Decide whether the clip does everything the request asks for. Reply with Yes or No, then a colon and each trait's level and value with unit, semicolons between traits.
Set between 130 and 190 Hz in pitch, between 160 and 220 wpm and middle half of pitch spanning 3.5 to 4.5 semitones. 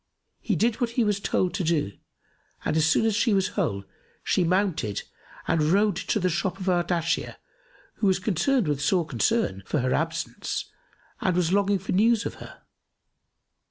Yes: medium, 185 Hz; average, 175 wpm; average, 4.2 semitones